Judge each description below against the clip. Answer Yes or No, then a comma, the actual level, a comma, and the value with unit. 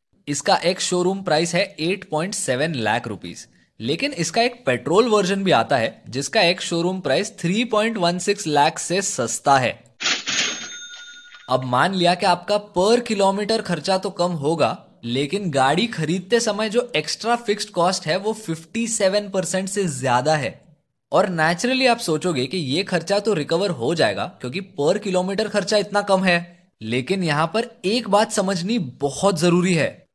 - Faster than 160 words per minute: No, average, 155 wpm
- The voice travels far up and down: No, average, 4.5 semitones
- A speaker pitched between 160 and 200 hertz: Yes, medium, 185 Hz